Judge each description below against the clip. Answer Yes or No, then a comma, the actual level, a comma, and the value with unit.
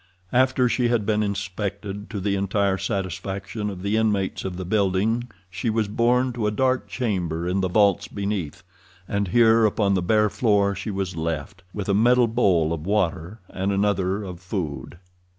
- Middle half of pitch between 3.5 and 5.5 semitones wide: No, average, 2.7 semitones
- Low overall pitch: Yes, low, 100 Hz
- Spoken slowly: No, average, 175 wpm